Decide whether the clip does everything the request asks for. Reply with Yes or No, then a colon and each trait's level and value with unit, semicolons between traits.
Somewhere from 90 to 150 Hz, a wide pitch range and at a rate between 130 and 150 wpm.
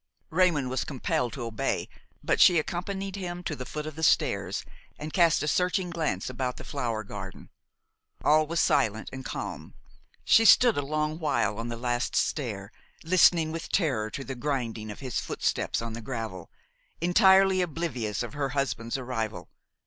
No: medium, 140 Hz; wide, 6.2 semitones; average, 170 wpm